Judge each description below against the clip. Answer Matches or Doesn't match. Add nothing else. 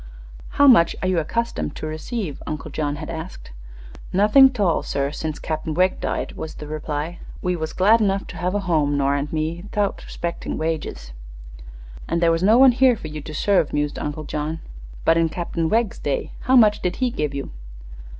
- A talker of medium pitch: Matches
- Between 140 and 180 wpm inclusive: Doesn't match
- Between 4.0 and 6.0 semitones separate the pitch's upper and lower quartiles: Matches